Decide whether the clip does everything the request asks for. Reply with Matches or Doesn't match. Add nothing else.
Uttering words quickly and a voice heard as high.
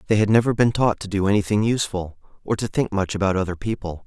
Doesn't match